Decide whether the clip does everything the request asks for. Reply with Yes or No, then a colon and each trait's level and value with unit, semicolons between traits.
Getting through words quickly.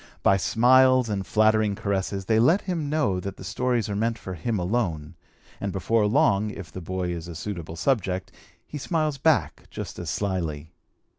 No: average, 175 wpm